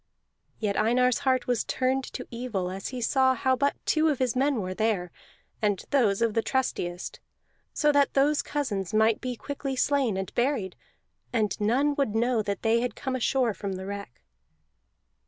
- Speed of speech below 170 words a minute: No, average, 175 wpm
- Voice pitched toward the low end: No, high, 240 Hz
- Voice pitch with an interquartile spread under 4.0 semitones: No, average, 4.3 semitones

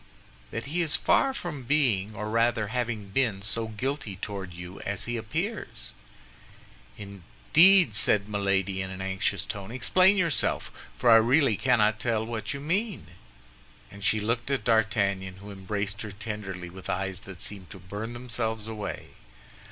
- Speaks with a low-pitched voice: Yes, low, 110 Hz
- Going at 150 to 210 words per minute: Yes, average, 155 wpm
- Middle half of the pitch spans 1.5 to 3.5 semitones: No, average, 3.9 semitones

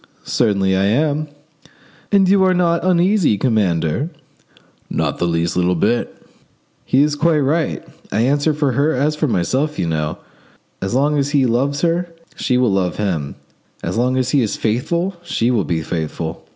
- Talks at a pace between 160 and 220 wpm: Yes, average, 175 wpm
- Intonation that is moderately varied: No, wide, 7.9 semitones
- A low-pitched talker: Yes, low, 130 Hz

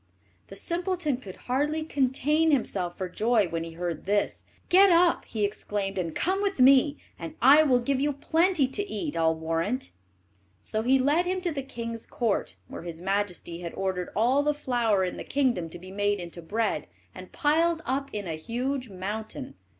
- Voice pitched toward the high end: Yes, high, 240 Hz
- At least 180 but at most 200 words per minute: Yes, average, 185 wpm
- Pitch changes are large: Yes, wide, 7.8 semitones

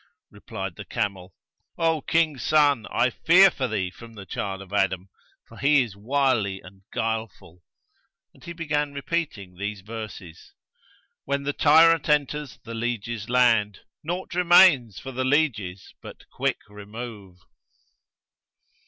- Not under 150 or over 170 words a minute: No, slow, 135 wpm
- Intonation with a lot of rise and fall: Yes, wide, 6.6 semitones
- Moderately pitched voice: No, low, 115 Hz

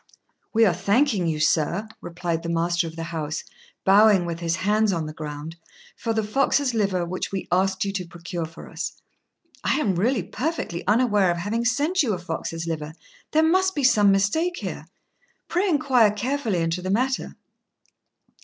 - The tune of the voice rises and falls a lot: Yes, wide, 5.8 semitones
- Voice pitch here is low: No, high, 195 Hz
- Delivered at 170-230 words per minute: Yes, average, 175 wpm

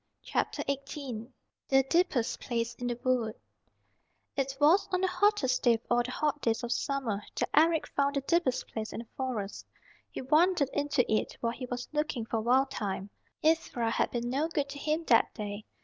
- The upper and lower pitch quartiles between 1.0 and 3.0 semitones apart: No, average, 4.1 semitones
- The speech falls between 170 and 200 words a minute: Yes, average, 190 wpm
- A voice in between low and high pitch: No, very high, 260 Hz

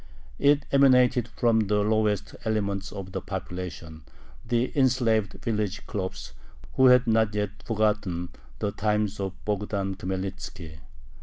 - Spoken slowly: Yes, slow, 125 wpm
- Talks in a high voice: No, low, 105 Hz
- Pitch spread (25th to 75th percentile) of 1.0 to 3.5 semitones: Yes, average, 2.9 semitones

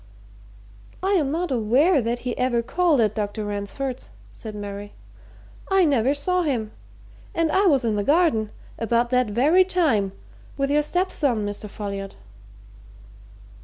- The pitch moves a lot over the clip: Yes, wide, 6.7 semitones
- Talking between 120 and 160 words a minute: Yes, average, 140 wpm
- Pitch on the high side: Yes, very high, 250 Hz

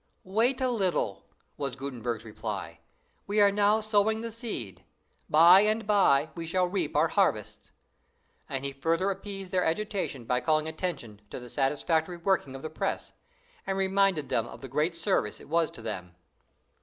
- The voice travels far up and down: Yes, wide, 6.6 semitones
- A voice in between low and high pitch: Yes, medium, 165 Hz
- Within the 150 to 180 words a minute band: Yes, average, 170 wpm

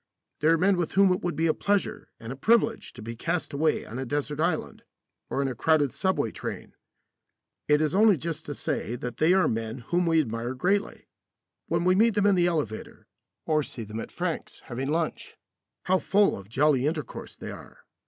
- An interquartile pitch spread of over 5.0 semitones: Yes, wide, 5.6 semitones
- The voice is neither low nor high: Yes, medium, 155 Hz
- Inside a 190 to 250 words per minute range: Yes, fast, 205 wpm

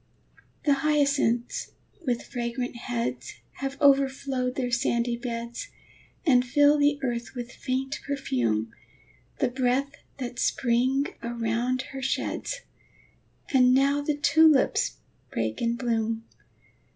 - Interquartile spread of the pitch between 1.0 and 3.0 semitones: Yes, average, 2.7 semitones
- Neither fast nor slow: No, slow, 110 wpm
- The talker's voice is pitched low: No, very high, 250 Hz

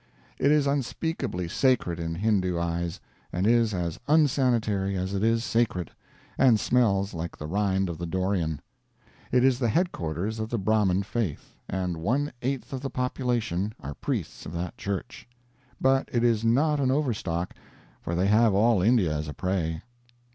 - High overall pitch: No, low, 105 Hz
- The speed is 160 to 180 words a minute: Yes, average, 165 wpm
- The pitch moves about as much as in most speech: No, wide, 5.7 semitones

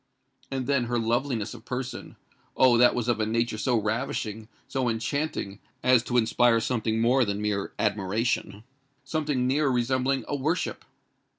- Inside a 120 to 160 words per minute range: Yes, average, 140 wpm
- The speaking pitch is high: No, low, 120 Hz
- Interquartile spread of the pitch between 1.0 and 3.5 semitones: Yes, average, 3.0 semitones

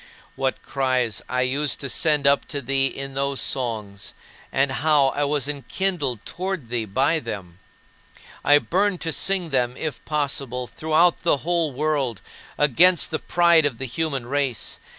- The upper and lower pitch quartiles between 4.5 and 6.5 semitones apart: No, average, 3.6 semitones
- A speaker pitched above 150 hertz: No, medium, 140 Hz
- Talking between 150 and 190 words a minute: Yes, average, 155 wpm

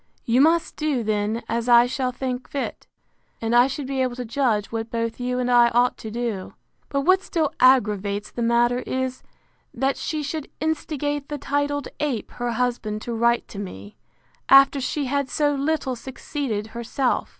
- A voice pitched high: Yes, very high, 250 Hz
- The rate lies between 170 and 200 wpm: Yes, average, 175 wpm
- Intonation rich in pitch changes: No, average, 3.3 semitones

